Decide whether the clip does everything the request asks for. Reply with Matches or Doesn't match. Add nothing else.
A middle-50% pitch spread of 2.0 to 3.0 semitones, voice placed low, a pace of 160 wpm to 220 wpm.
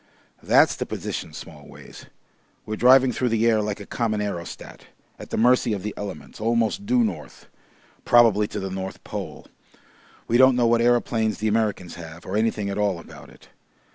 Matches